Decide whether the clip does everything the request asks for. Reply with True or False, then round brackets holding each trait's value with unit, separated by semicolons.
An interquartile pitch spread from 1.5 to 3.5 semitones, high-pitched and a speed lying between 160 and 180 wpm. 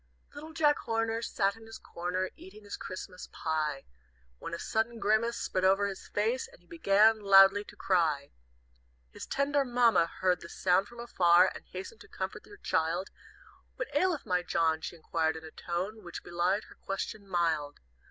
False (4.6 semitones; 195 Hz; 175 wpm)